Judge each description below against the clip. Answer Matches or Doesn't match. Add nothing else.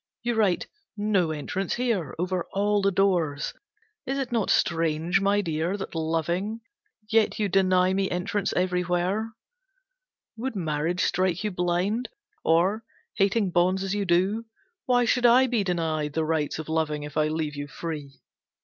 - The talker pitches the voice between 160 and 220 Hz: Matches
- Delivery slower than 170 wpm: Matches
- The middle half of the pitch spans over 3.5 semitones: Matches